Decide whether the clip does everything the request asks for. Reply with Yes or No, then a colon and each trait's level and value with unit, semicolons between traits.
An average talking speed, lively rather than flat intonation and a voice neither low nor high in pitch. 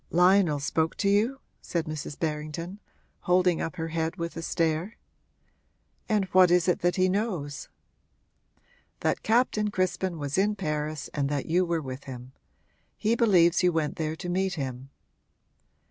No: average, 155 wpm; average, 3.5 semitones; medium, 170 Hz